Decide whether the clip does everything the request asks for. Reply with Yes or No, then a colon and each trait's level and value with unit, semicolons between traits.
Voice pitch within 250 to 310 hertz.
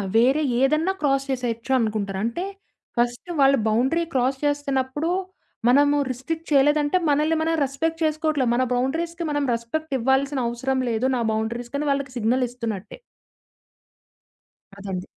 Yes: very high, 270 Hz